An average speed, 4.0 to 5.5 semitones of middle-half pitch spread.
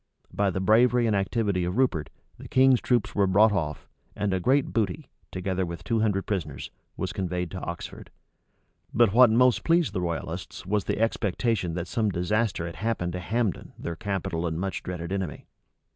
Yes: average, 180 wpm; average, 4.4 semitones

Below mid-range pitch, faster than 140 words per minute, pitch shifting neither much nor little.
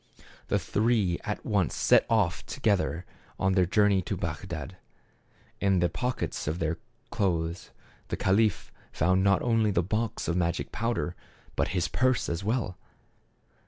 Yes: very low, 95 Hz; average, 150 wpm; average, 3.8 semitones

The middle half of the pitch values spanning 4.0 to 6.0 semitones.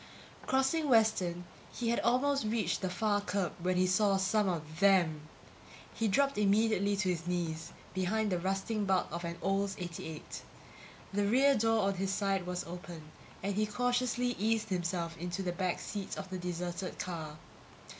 No: average, 3.5 semitones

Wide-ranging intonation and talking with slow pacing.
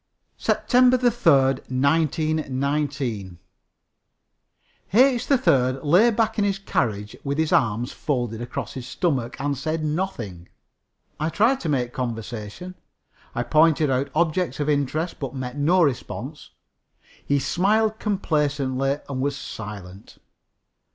Yes: wide, 5.7 semitones; slow, 115 wpm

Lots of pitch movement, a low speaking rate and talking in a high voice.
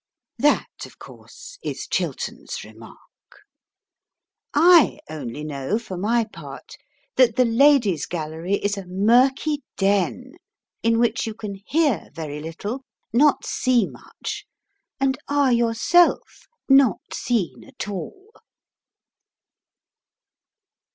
Yes: wide, 6.2 semitones; slow, 105 wpm; high, 230 Hz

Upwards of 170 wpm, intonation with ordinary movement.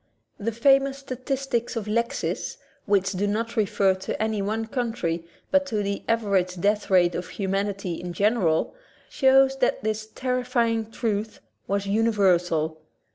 No: average, 140 wpm; average, 3.3 semitones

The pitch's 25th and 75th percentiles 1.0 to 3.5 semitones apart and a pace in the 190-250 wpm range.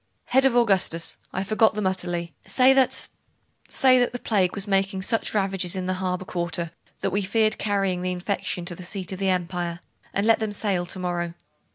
Yes: average, 3.0 semitones; average, 200 wpm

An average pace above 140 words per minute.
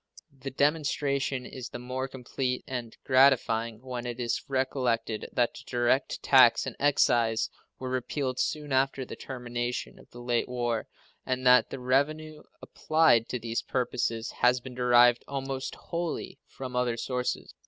Yes: average, 150 wpm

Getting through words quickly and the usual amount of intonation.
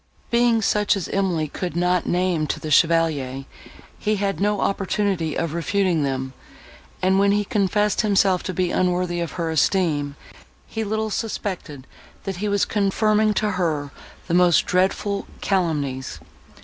No: average, 150 wpm; average, 3.8 semitones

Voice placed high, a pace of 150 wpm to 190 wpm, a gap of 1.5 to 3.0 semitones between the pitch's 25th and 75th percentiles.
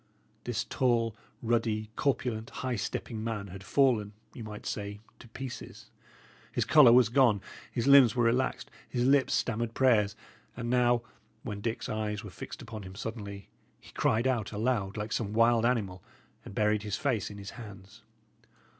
No: low, 115 Hz; average, 165 wpm; average, 2.7 semitones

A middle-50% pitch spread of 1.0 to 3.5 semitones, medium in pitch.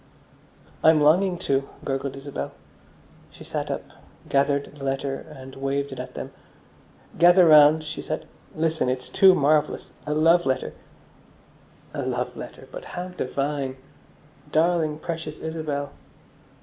Yes: average, 2.8 semitones; medium, 150 Hz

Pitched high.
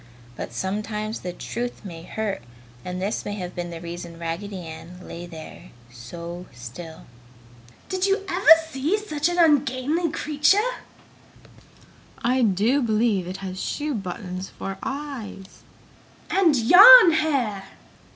Yes: high, 210 Hz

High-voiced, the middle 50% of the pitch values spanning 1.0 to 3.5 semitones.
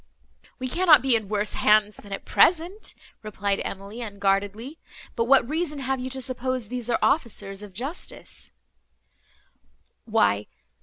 No: high, 235 Hz; average, 4.6 semitones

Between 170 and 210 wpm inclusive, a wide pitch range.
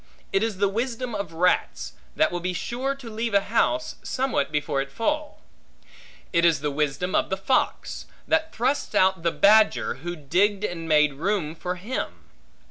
Yes: average, 175 wpm; wide, 5.8 semitones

